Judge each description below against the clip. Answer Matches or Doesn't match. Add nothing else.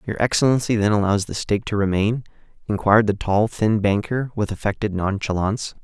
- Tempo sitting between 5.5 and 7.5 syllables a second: Matches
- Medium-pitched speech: Doesn't match